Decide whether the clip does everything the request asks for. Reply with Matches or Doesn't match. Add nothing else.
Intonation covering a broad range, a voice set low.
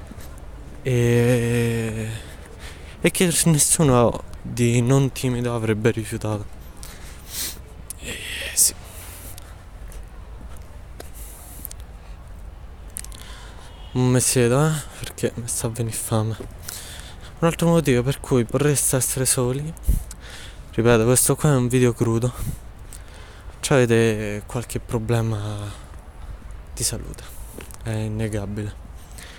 Matches